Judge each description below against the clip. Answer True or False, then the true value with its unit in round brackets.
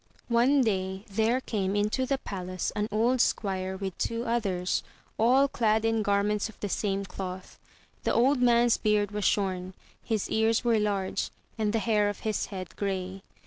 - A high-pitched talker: True (210 Hz)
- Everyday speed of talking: True (170 wpm)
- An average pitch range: True (3.0 semitones)